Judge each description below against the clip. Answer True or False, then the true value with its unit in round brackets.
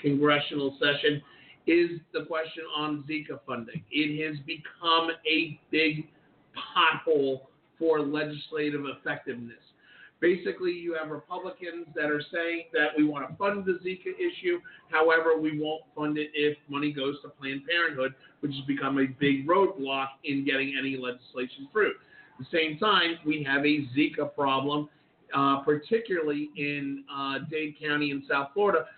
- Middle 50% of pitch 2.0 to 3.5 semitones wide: True (2.6 semitones)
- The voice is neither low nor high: True (150 Hz)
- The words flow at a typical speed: True (150 wpm)